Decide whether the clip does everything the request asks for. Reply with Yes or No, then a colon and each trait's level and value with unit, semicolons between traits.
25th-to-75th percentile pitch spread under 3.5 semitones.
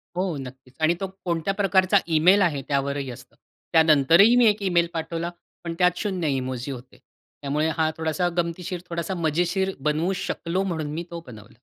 No: average, 4.0 semitones